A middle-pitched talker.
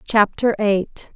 No: high, 210 Hz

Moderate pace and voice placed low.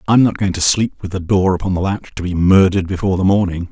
No: fast, 275 wpm; very low, 95 Hz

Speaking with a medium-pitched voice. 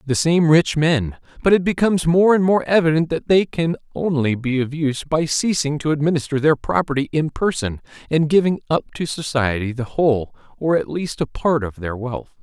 Yes: medium, 150 Hz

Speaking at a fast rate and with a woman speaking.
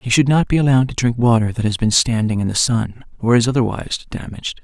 No: fast, 245 wpm; male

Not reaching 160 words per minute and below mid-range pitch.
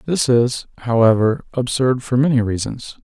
Yes: slow, 135 wpm; low, 125 Hz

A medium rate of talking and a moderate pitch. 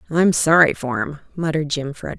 Yes: average, 165 wpm; medium, 150 Hz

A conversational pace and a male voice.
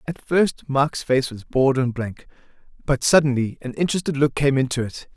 Yes: average, 185 wpm; male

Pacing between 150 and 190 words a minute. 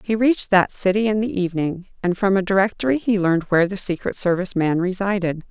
No: fast, 205 wpm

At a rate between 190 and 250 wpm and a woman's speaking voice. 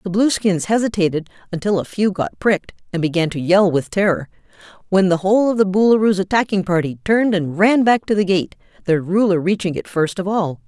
Yes: average, 200 wpm; female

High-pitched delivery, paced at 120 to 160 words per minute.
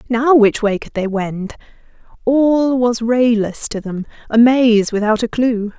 Yes: high, 230 Hz; average, 155 wpm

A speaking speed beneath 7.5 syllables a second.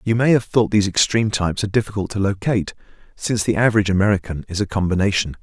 No: 7.6 syllables/s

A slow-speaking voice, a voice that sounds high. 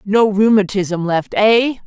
Yes: slow, 130 wpm; high, 205 Hz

